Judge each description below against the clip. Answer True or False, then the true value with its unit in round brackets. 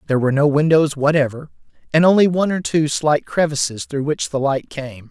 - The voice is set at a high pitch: False (145 Hz)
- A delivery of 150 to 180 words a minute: False (200 wpm)